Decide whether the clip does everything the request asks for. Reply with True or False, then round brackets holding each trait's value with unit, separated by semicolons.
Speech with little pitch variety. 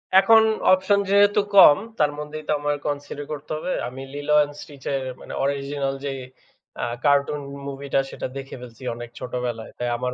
True (2.3 semitones)